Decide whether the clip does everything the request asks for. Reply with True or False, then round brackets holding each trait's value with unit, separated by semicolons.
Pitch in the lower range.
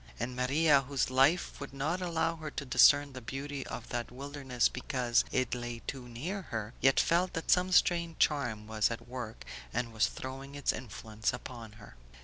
True (130 Hz)